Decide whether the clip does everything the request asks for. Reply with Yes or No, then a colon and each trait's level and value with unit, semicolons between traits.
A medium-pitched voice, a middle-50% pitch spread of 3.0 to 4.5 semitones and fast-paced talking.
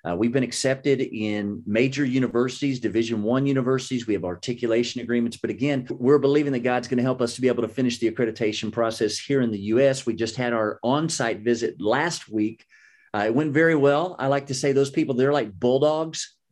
No: low, 125 Hz; average, 3.3 semitones; fast, 210 wpm